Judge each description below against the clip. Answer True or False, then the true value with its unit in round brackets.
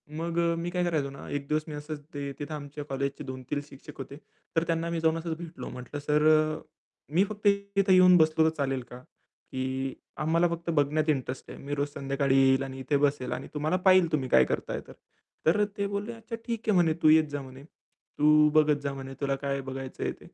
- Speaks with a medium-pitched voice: True (150 Hz)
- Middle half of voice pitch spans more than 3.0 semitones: True (3.4 semitones)